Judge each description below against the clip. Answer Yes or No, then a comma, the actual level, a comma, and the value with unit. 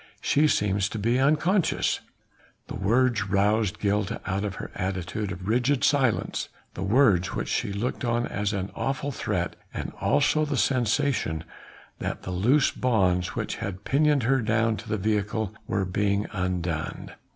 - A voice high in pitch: No, low, 105 Hz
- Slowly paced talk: No, average, 155 wpm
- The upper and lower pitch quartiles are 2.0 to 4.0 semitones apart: No, average, 4.8 semitones